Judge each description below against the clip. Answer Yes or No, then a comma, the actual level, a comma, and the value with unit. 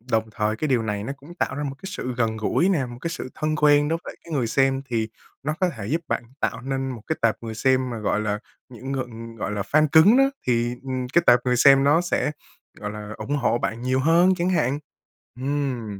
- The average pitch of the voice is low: Yes, low, 130 Hz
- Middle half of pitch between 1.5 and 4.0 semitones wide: No, average, 4.6 semitones